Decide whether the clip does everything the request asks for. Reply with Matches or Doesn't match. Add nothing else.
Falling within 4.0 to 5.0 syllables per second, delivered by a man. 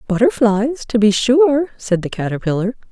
Doesn't match